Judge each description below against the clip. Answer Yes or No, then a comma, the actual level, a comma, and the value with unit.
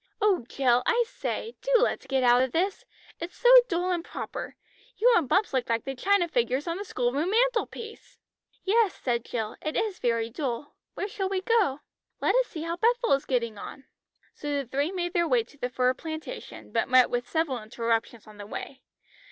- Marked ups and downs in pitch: Yes, wide, 8.1 semitones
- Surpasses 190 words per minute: Yes, average, 200 wpm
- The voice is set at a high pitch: Yes, very high, 310 Hz